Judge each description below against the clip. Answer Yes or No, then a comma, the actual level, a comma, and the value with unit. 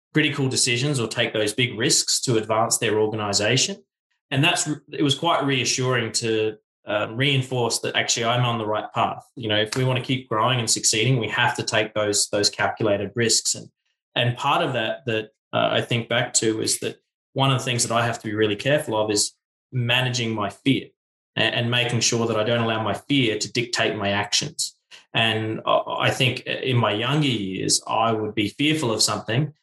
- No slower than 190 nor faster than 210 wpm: Yes, fast, 205 wpm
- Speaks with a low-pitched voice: Yes, low, 115 Hz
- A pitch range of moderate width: Yes, average, 3.1 semitones